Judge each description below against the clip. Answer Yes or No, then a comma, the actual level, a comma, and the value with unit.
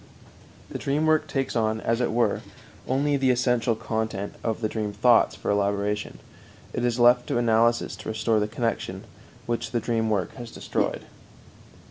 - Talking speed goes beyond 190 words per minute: No, average, 165 wpm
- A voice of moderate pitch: No, low, 115 Hz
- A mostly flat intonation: Yes, narrow, 2.1 semitones